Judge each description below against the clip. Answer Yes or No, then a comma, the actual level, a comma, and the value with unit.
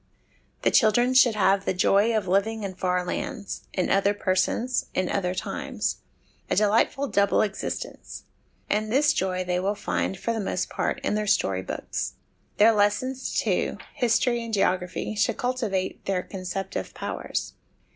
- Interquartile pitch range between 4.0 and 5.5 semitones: No, average, 3.3 semitones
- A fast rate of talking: No, average, 155 wpm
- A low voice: No, high, 205 Hz